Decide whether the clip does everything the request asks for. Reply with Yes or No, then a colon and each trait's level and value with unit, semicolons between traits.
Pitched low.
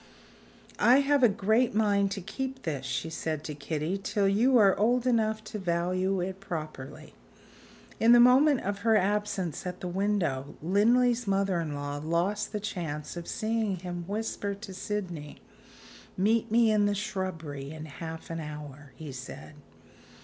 No: high, 195 Hz